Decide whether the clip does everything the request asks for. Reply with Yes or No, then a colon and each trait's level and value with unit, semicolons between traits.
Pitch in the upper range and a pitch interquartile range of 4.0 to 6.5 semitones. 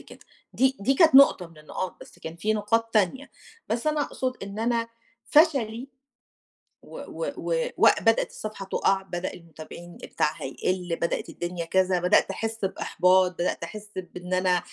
Yes: high, 195 Hz; average, 4.5 semitones